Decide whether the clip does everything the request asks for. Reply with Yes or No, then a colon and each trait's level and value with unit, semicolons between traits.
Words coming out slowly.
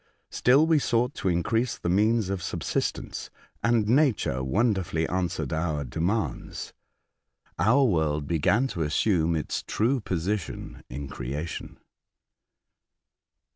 Yes: slow, 110 wpm